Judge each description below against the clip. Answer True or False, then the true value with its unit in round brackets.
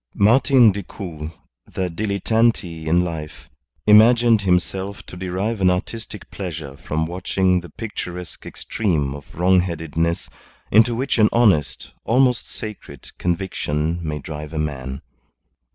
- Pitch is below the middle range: True (90 Hz)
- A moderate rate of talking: False (120 wpm)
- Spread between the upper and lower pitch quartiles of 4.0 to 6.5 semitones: True (5.0 semitones)